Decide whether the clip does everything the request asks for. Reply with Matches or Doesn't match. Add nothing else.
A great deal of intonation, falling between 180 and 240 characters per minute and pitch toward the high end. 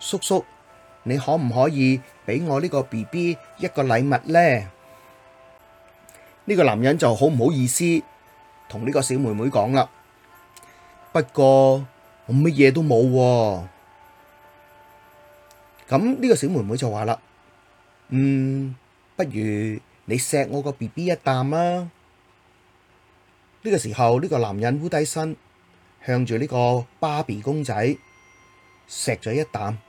Doesn't match